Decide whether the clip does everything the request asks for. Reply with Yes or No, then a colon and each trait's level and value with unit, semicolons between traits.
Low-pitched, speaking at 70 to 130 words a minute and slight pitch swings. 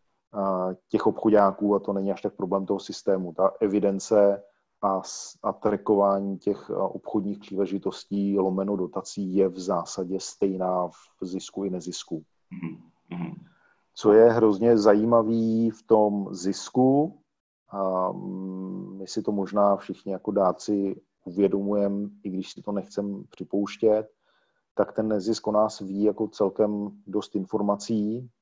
Yes: low, 100 Hz; average, 125 wpm; narrow, 1.6 semitones